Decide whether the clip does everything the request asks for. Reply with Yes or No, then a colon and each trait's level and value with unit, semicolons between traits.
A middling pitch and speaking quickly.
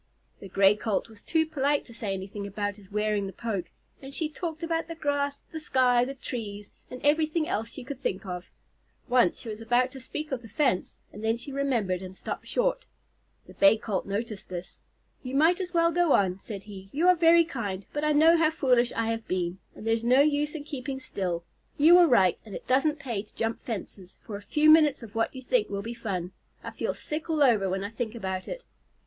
No: high, 240 Hz; fast, 230 wpm